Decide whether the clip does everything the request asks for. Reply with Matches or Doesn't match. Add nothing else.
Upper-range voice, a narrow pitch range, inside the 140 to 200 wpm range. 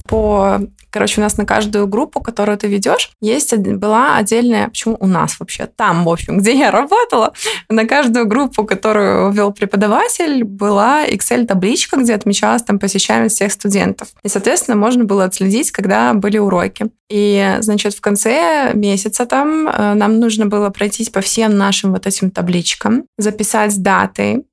Matches